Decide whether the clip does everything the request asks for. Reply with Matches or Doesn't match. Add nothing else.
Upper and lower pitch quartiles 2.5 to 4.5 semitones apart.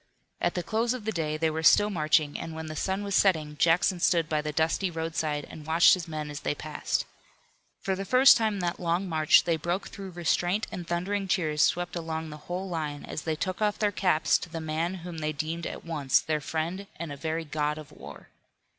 Matches